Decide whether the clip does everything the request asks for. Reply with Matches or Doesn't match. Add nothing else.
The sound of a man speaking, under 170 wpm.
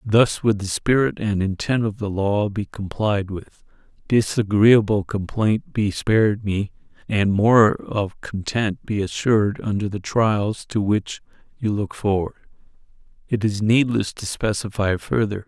Matches